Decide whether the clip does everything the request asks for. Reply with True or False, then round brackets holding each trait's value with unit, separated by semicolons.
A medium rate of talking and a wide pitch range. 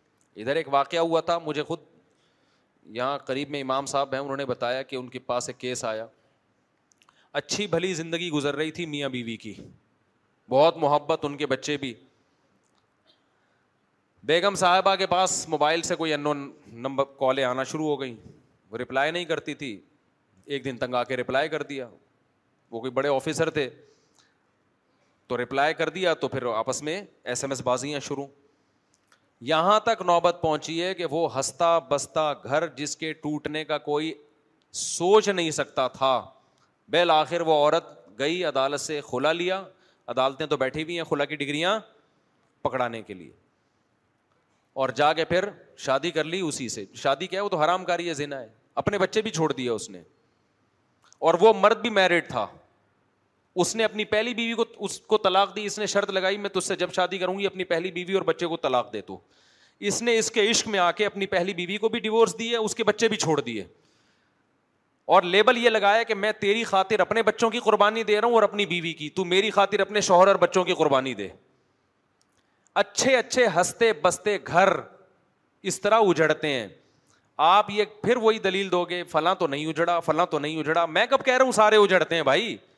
False (195 wpm; 5.8 semitones)